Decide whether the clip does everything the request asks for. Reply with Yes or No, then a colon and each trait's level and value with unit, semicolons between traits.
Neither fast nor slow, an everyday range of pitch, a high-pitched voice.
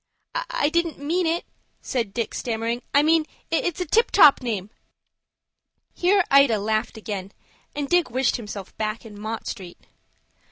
No: average, 150 wpm; wide, 6.9 semitones; high, 245 Hz